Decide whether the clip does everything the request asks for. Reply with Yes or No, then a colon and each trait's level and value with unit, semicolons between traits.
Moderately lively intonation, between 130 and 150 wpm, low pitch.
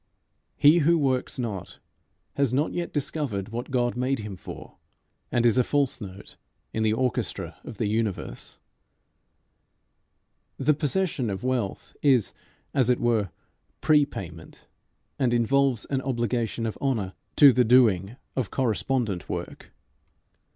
Yes: average, 4.0 semitones; slow, 135 wpm; low, 125 Hz